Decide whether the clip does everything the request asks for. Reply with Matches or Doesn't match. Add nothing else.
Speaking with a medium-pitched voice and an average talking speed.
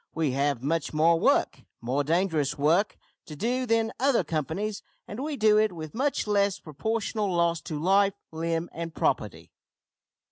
Matches